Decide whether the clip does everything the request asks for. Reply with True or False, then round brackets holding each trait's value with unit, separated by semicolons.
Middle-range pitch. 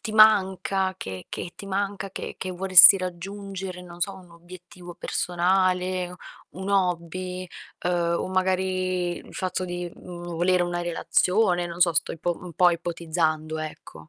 True (180 Hz)